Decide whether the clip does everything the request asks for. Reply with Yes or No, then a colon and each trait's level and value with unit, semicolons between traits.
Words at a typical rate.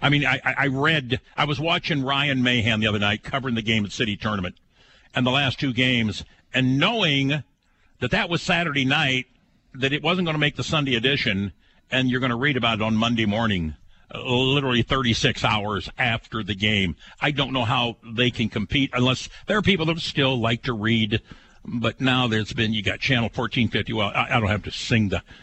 No: fast, 210 wpm